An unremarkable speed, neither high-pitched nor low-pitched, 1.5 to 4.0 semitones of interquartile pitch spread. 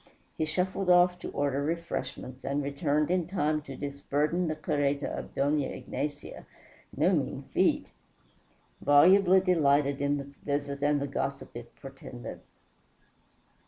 No: slow, 130 wpm; medium, 145 Hz; average, 2.8 semitones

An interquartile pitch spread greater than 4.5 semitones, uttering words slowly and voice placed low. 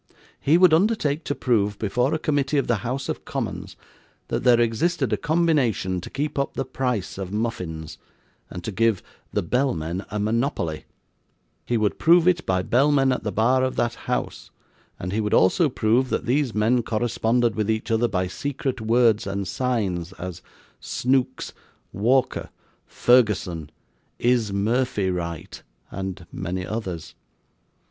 No: average, 5.1 semitones; average, 155 wpm; low, 115 Hz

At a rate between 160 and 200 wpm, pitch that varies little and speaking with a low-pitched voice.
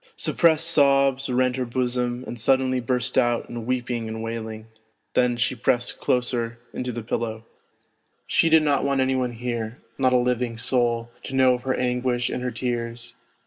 Yes: average, 180 wpm; narrow, 1.7 semitones; low, 125 Hz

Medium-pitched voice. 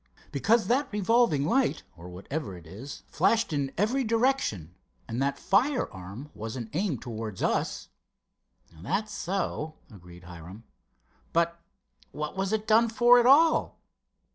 Yes: medium, 160 Hz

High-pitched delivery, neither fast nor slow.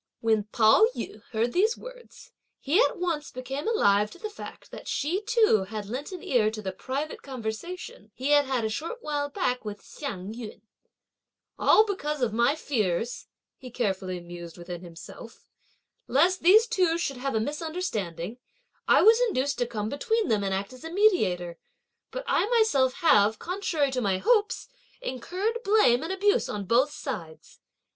Yes: very high, 265 Hz; average, 170 wpm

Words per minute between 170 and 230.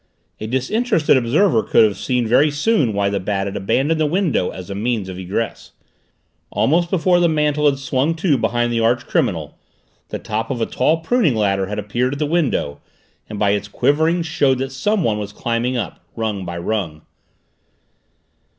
Yes: average, 180 wpm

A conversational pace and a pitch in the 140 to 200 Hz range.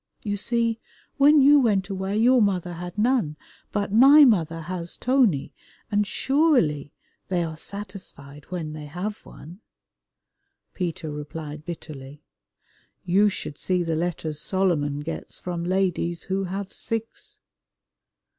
No: slow, 125 wpm; medium, 185 Hz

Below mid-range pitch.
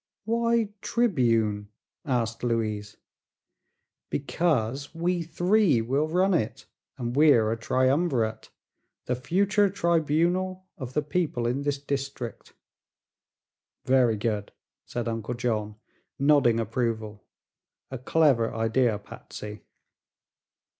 Yes: low, 130 Hz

